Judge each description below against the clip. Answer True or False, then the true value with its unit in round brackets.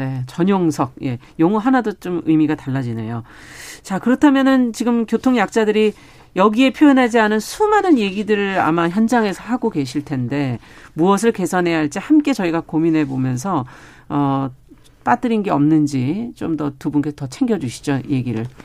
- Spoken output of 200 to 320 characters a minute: False (330 characters per minute)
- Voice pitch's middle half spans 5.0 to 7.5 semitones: False (8.2 semitones)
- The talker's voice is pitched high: False (170 Hz)